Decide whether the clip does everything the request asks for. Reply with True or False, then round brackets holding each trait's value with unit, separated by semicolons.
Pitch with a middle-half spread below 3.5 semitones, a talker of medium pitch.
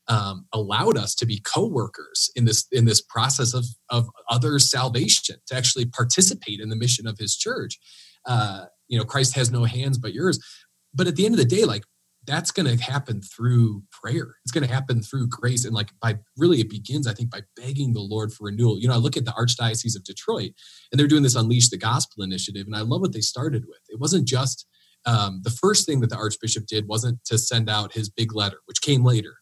False (2.9 semitones; 120 Hz)